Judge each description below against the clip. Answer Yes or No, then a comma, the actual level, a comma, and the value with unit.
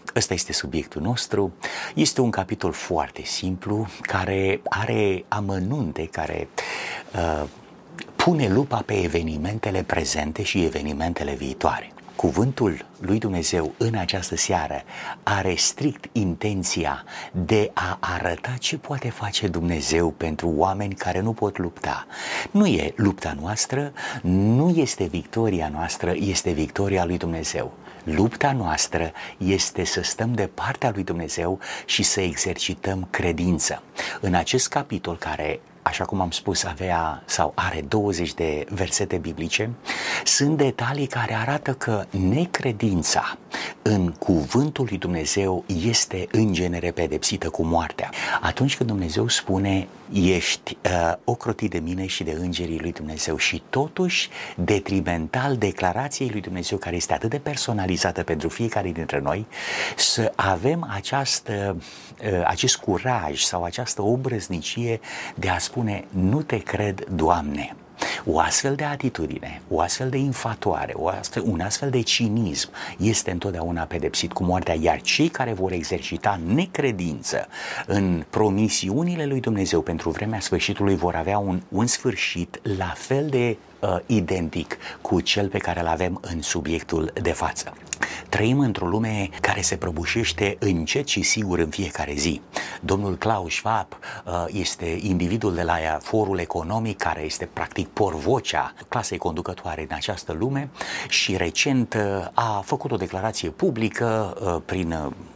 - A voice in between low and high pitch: No, very low, 95 Hz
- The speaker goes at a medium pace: Yes, average, 135 wpm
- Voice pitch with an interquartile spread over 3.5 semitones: Yes, average, 4.6 semitones